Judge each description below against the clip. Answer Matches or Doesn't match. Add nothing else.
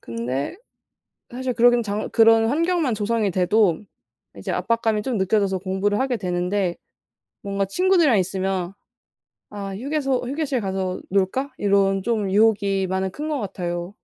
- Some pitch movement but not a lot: Matches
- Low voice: Doesn't match